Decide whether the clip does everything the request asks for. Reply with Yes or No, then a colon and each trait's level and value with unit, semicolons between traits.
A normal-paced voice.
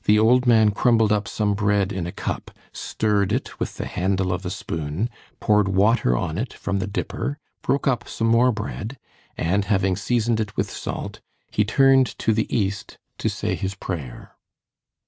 Yes: average, 180 wpm